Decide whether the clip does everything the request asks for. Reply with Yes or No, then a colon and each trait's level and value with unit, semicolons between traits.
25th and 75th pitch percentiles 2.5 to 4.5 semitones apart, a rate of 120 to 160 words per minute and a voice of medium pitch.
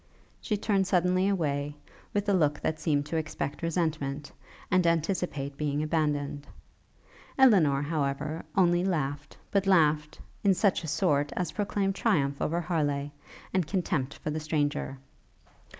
Yes: average, 4.1 semitones; slow, 135 wpm; medium, 155 Hz